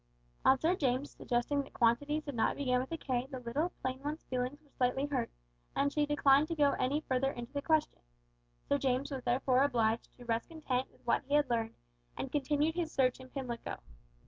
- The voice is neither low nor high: No, very high, 270 Hz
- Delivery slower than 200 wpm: No, fast, 205 wpm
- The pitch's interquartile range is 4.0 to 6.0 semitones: No, average, 2.7 semitones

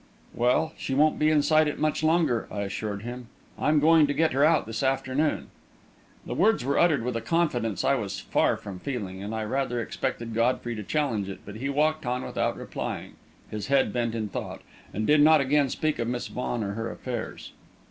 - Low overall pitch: Yes, low, 125 Hz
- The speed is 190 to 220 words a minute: Yes, fast, 205 wpm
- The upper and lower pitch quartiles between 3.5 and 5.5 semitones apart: Yes, average, 5.0 semitones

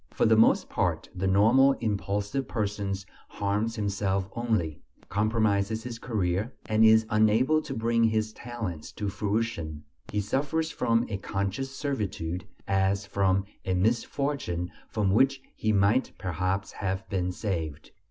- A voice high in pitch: No, low, 105 Hz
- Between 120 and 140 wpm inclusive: Yes, slow, 135 wpm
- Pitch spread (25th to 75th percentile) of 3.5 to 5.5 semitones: No, average, 3.0 semitones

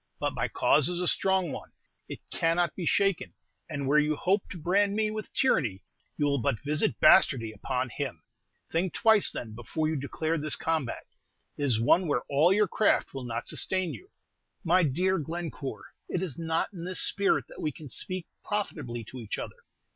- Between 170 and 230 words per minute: Yes, average, 190 wpm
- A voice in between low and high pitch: Yes, medium, 160 Hz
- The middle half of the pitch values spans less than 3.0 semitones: No, wide, 5.4 semitones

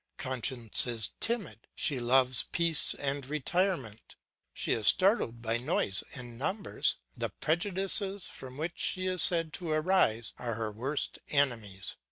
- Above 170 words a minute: No, average, 140 wpm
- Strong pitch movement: Yes, wide, 6.9 semitones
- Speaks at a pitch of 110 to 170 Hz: Yes, medium, 140 Hz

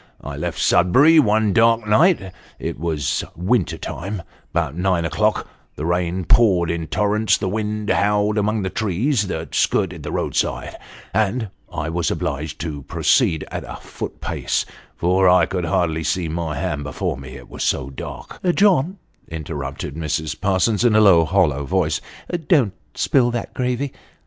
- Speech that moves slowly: No, average, 165 wpm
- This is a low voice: Yes, very low, 95 Hz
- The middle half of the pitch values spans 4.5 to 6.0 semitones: Yes, average, 5.1 semitones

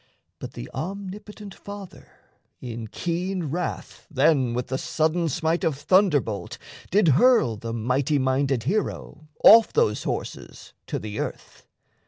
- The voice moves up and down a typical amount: No, wide, 6.8 semitones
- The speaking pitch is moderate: Yes, medium, 155 Hz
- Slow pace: Yes, slow, 130 wpm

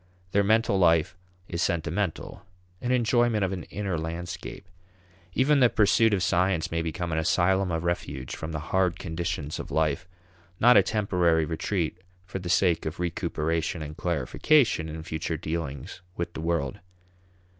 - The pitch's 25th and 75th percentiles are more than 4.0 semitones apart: No, average, 3.4 semitones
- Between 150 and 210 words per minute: Yes, average, 155 wpm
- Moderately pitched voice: No, very low, 85 Hz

